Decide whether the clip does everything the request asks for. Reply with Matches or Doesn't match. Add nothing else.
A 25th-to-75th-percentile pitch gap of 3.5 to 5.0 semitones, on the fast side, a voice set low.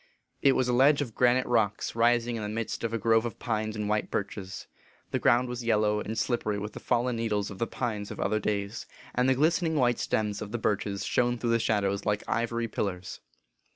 Doesn't match